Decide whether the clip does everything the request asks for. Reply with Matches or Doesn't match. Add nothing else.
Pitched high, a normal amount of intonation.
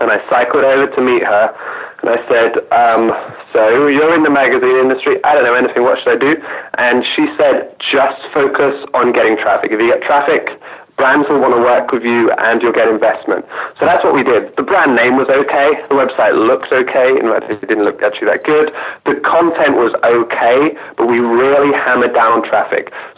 Doesn't match